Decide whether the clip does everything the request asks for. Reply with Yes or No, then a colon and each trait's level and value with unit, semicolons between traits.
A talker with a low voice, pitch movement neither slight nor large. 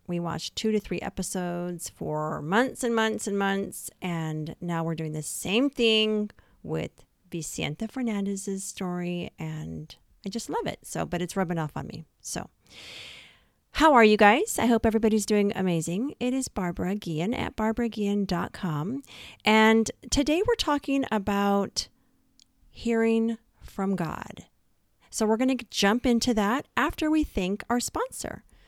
No: high, 205 Hz; average, 4.7 semitones